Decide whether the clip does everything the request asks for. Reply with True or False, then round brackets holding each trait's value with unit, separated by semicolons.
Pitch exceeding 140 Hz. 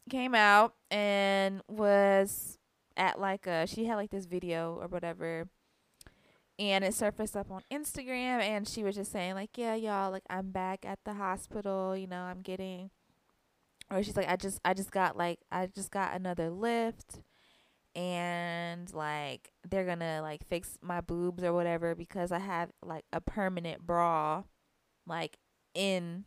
True (190 Hz)